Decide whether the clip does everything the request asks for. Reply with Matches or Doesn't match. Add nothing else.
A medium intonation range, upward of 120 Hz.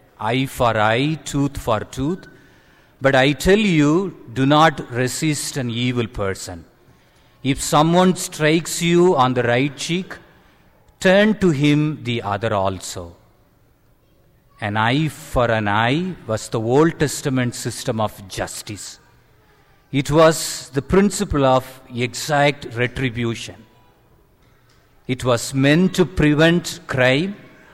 Matches